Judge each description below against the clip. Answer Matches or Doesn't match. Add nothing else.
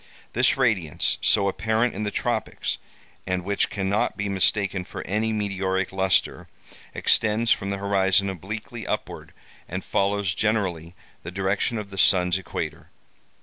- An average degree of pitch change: Doesn't match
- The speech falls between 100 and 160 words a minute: Matches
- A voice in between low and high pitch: Doesn't match